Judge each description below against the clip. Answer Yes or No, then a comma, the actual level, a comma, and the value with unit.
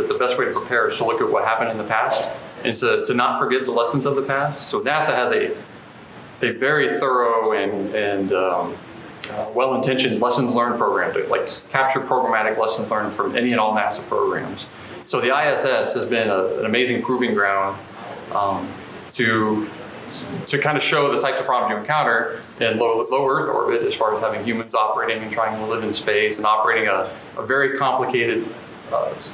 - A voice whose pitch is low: Yes, low, 120 Hz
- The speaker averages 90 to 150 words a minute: No, average, 200 wpm